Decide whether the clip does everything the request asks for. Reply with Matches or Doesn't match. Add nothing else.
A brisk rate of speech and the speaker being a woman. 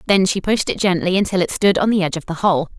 Matches